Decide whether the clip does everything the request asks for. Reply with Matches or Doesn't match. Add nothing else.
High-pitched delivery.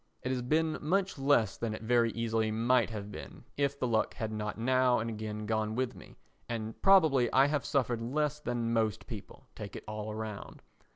Doesn't match